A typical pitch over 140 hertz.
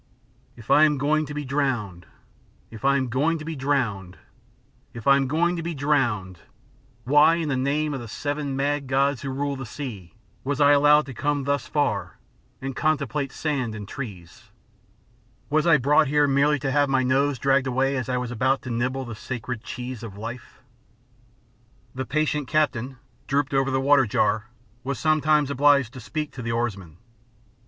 No: low, 135 Hz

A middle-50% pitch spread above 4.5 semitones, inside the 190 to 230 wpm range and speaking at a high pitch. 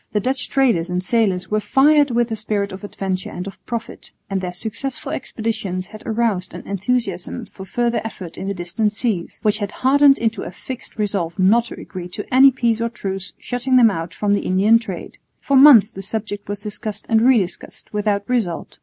No: average, 3.7 semitones; average, 200 wpm; high, 215 Hz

